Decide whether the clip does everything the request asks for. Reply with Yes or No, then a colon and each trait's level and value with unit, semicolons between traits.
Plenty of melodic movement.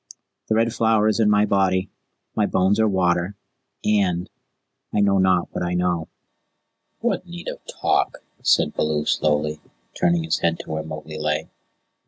No: average, 4.6 semitones